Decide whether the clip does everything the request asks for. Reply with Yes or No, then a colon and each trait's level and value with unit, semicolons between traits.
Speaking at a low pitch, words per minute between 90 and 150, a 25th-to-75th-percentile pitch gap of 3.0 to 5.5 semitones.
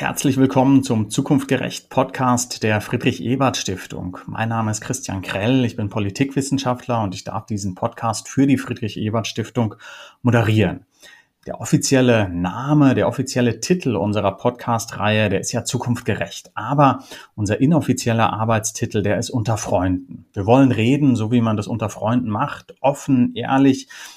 Yes: low, 120 Hz; average, 140 wpm; average, 3.4 semitones